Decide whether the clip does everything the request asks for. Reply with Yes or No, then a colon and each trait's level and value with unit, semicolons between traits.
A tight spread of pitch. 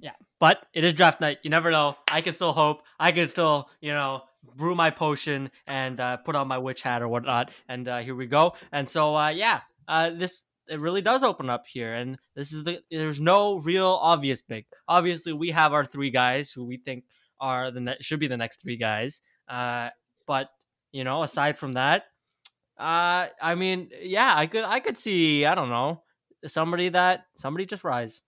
No: average, 4.4 semitones